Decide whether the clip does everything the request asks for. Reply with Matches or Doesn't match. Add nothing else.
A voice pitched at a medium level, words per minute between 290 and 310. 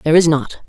Doesn't match